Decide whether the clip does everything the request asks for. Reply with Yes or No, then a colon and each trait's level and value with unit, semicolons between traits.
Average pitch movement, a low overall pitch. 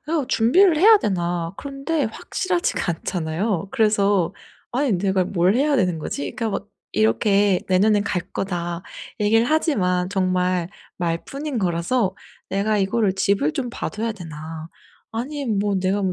No: average, 4.7 semitones; high, 200 Hz